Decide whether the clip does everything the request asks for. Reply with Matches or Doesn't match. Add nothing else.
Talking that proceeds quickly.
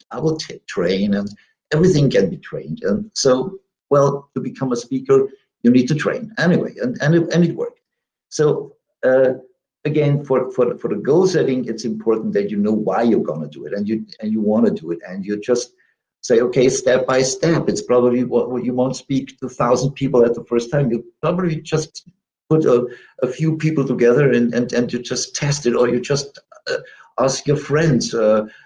Matches